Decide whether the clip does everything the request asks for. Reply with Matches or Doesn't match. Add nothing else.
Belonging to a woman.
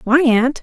Matches